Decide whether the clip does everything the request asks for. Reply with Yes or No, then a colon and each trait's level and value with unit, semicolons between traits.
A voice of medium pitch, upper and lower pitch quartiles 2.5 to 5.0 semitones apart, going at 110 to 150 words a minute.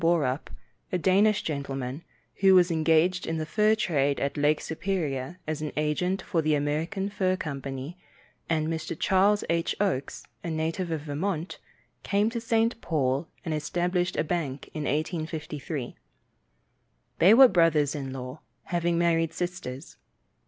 Yes: medium, 165 Hz; average, 3.8 semitones; average, 145 wpm